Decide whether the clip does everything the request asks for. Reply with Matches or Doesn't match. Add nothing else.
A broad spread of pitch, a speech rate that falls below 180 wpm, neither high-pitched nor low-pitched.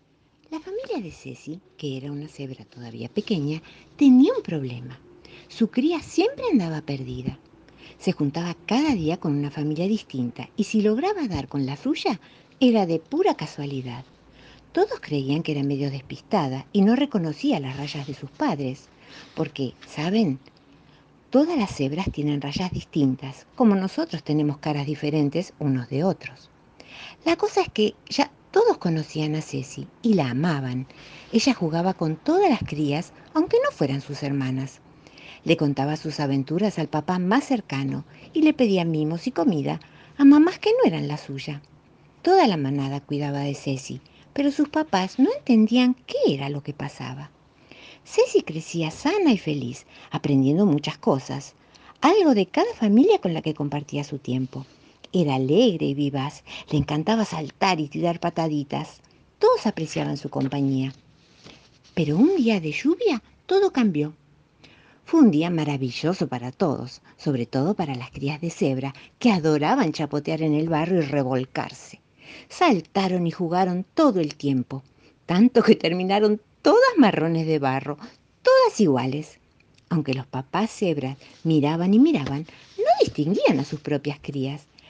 Matches